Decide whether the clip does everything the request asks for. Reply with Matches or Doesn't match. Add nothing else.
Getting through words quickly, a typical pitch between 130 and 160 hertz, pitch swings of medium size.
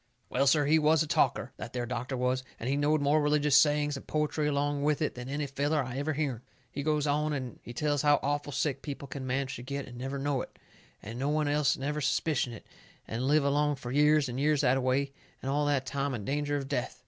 Doesn't match